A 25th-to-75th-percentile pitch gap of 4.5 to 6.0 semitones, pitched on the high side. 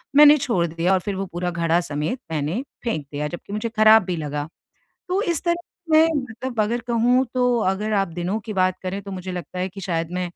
Yes: wide, 5.6 semitones; high, 195 Hz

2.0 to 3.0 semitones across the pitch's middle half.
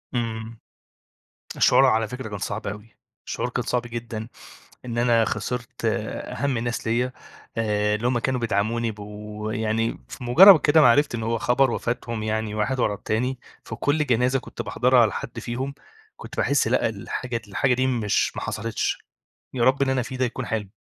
Yes: narrow, 2.6 semitones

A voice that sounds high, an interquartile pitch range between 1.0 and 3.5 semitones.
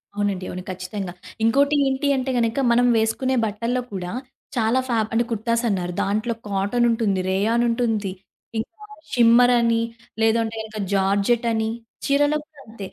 Yes: high, 225 Hz; average, 3.1 semitones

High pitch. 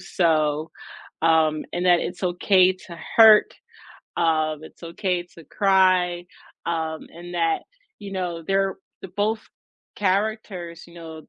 No: medium, 175 Hz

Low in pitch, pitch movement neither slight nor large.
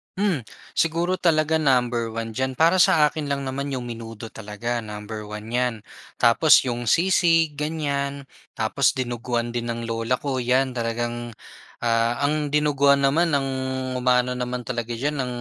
Yes: low, 125 Hz; average, 3.9 semitones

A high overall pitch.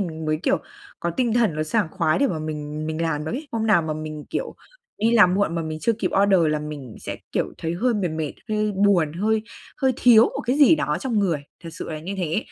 No: medium, 175 Hz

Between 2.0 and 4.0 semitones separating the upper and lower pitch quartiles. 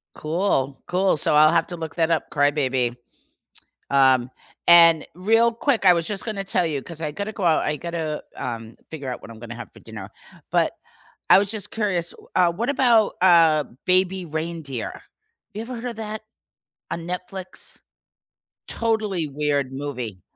No: average, 5.3 semitones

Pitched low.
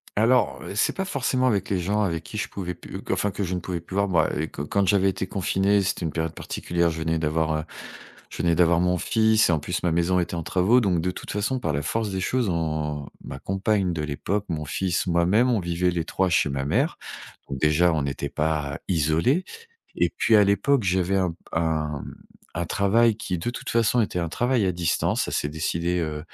Yes: very low, 90 Hz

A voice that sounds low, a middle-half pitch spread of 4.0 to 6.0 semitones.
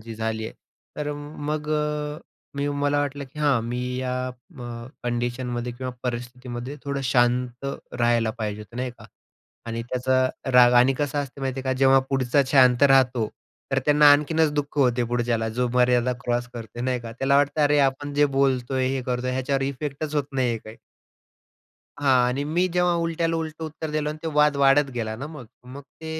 No: low, 130 Hz; average, 2.9 semitones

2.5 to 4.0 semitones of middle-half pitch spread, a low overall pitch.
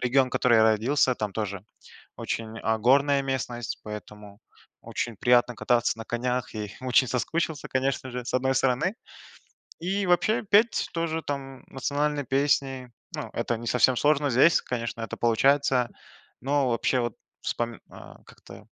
Yes: average, 3.2 semitones; low, 125 Hz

